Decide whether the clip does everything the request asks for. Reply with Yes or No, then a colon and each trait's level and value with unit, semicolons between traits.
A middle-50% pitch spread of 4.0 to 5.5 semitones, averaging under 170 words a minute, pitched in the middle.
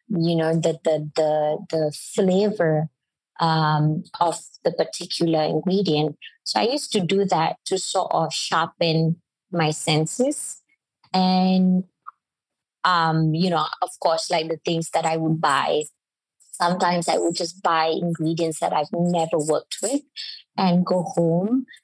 No: narrow, 2.6 semitones; average, 140 wpm; medium, 170 Hz